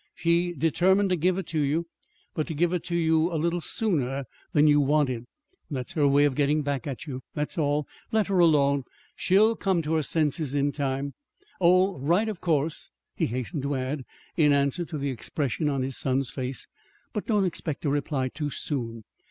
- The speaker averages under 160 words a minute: No, average, 195 wpm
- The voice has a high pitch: No, medium, 150 Hz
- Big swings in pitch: No, average, 3.7 semitones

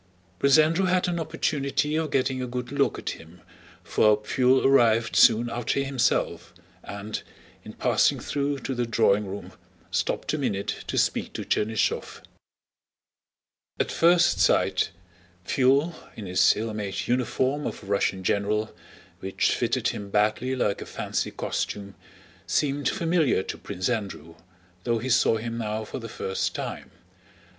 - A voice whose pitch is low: Yes, low, 120 Hz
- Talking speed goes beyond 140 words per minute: Yes, average, 150 wpm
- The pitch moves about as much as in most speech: Yes, average, 4.7 semitones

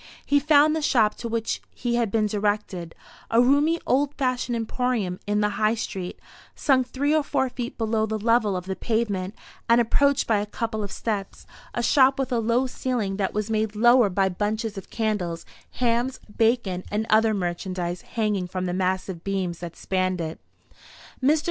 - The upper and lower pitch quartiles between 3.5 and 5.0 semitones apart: Yes, average, 4.1 semitones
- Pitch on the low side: No, high, 220 Hz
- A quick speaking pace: No, average, 180 wpm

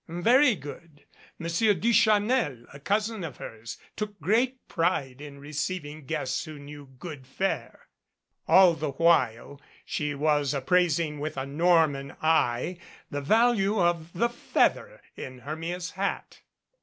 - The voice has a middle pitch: Yes, medium, 165 Hz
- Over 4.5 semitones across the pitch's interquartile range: Yes, wide, 5.4 semitones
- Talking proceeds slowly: Yes, slow, 130 wpm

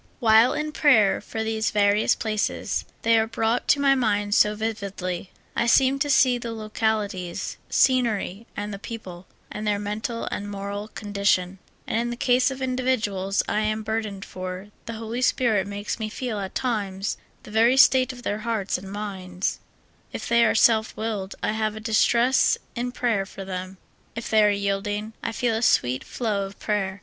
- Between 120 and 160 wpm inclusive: No, average, 180 wpm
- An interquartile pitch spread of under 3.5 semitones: Yes, narrow, 2.6 semitones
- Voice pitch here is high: Yes, high, 215 Hz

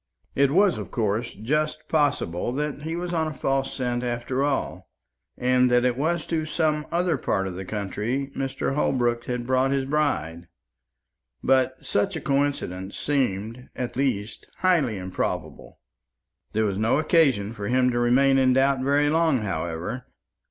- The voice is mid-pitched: No, low, 130 Hz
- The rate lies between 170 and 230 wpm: No, average, 160 wpm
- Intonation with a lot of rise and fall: No, average, 4.2 semitones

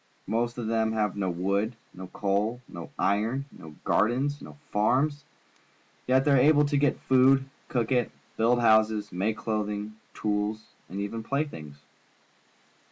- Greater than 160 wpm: No, average, 145 wpm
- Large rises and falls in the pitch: No, average, 4.0 semitones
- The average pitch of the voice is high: No, low, 110 Hz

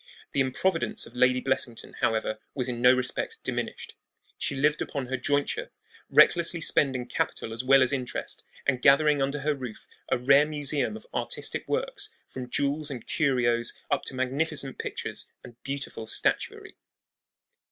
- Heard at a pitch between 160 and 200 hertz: No, low, 135 Hz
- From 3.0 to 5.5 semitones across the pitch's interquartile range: No, narrow, 2.5 semitones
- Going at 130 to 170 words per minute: Yes, average, 150 wpm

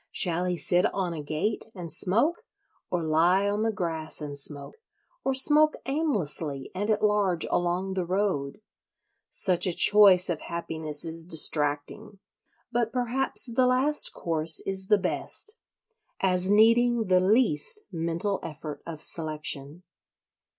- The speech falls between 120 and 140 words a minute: Yes, slow, 135 wpm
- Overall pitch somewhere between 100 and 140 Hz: No, medium, 185 Hz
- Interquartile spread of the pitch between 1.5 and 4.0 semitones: No, average, 5.1 semitones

